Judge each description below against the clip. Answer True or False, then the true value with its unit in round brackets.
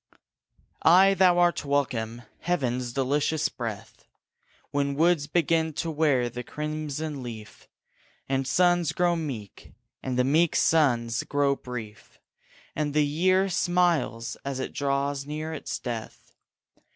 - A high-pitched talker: False (145 Hz)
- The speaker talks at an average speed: False (125 wpm)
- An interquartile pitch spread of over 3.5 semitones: True (4.4 semitones)